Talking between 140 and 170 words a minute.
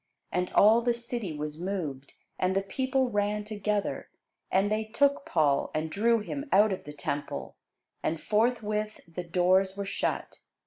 Yes: average, 160 wpm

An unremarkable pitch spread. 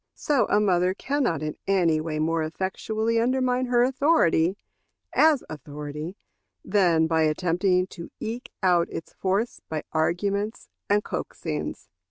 No: wide, 5.9 semitones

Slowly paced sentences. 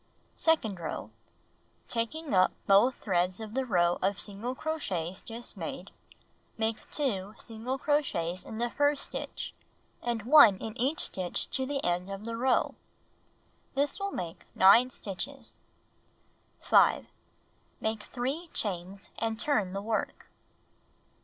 Yes: slow, 130 wpm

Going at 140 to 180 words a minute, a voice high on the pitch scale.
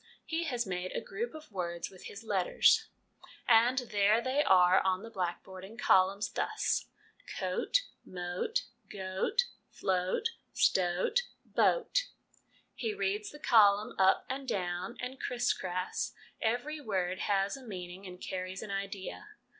Yes: average, 160 wpm; high, 200 Hz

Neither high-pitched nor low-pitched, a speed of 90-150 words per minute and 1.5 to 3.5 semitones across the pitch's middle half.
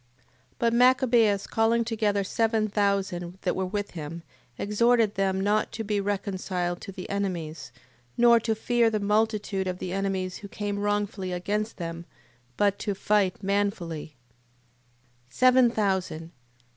No: high, 200 Hz; average, 140 wpm; average, 2.8 semitones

